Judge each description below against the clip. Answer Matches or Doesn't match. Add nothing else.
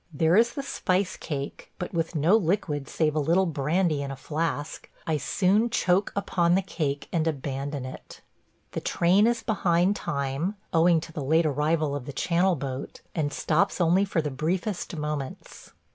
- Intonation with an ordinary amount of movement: Matches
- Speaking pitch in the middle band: Matches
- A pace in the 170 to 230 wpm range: Matches